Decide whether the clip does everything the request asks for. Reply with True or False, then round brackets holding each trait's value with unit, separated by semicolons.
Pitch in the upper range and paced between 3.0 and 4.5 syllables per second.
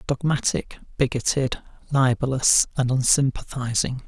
False (130 Hz; 4.4 syllables/s)